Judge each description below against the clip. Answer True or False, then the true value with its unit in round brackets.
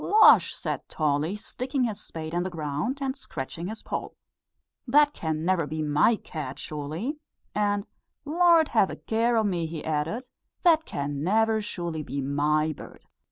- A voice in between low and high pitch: True (175 Hz)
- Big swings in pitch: True (7.4 semitones)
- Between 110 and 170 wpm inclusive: True (160 wpm)